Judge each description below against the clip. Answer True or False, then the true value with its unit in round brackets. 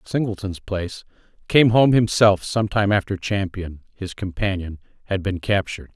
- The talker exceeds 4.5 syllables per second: True (5.2 syllables/s)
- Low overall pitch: True (100 Hz)